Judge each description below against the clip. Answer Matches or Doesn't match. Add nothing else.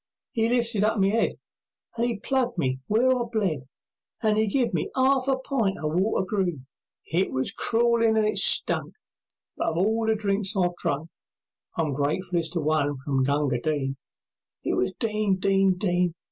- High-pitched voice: Matches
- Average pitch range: Doesn't match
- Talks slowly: Doesn't match